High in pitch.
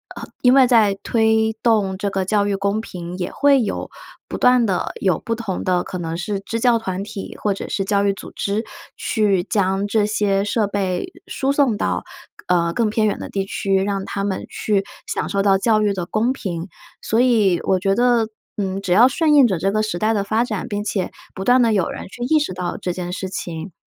Yes: high, 205 Hz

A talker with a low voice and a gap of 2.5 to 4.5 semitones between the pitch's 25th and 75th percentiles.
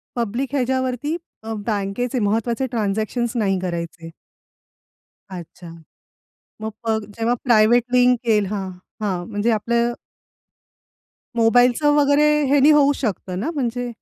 No: high, 235 Hz; average, 3.5 semitones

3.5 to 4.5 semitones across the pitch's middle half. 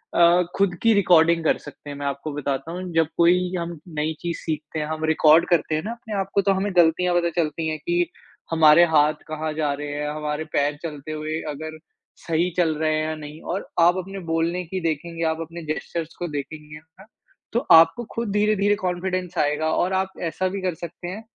No: average, 2.7 semitones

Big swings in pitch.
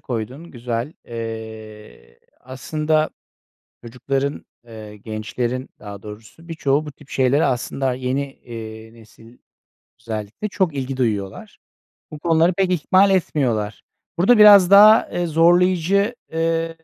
Yes: wide, 6.6 semitones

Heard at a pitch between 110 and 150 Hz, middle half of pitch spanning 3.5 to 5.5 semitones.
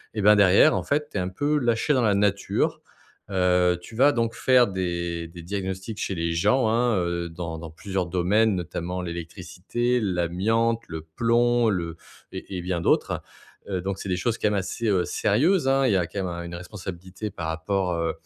No: very low, 95 Hz; average, 4.5 semitones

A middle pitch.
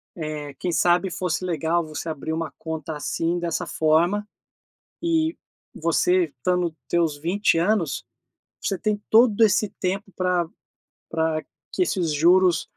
Yes: medium, 175 Hz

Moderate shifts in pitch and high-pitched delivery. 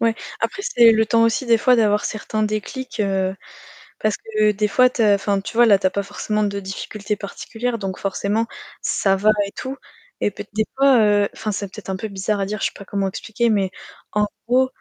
No: narrow, 2.3 semitones; high, 210 Hz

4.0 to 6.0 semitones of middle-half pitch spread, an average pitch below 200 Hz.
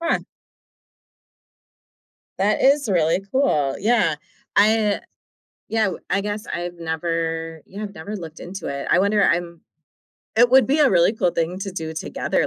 Yes: average, 4.5 semitones; high, 190 Hz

